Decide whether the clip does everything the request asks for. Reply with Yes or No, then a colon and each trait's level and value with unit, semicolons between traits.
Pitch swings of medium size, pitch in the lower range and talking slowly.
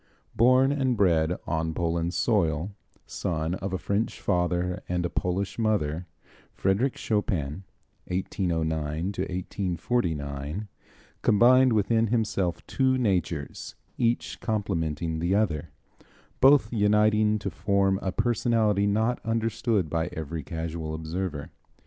Yes: average, 4.8 semitones; very low, 95 Hz; slow, 110 wpm